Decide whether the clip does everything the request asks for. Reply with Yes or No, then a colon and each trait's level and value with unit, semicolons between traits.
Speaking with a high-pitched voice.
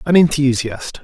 No: medium, 140 Hz